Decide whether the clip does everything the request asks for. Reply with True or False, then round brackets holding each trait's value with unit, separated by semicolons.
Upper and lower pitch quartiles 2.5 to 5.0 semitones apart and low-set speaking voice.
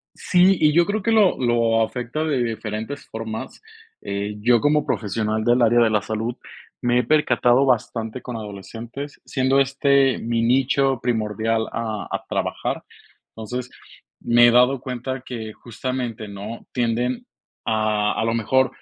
True (2.9 semitones; 120 Hz)